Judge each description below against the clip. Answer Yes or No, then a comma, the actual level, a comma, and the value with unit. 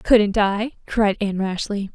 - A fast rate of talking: No, average, 155 wpm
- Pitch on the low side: No, high, 205 Hz